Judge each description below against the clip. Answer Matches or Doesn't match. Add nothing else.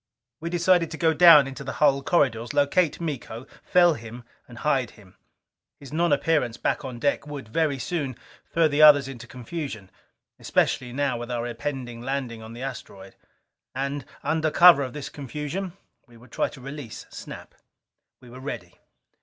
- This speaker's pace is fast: Doesn't match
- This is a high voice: Doesn't match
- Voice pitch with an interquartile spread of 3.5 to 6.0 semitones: Matches